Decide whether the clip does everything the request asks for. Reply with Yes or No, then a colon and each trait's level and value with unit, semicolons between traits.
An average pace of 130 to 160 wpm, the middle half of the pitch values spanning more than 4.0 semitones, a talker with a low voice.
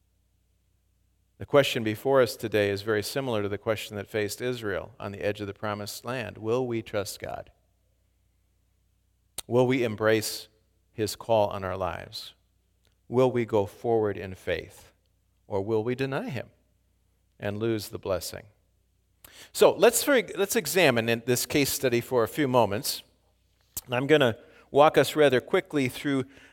Yes: average, 155 wpm; average, 4.6 semitones; low, 105 Hz